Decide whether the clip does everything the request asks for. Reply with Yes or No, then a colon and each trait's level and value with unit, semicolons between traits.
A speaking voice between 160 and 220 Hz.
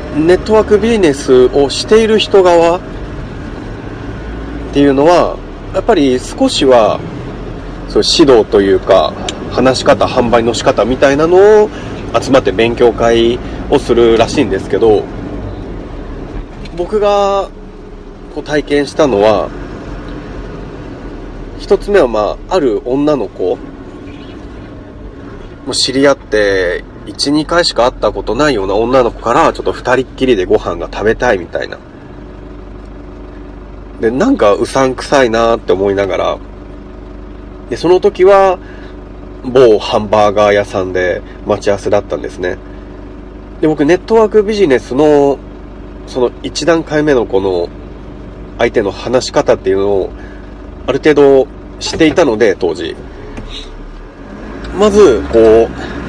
No: low, 125 Hz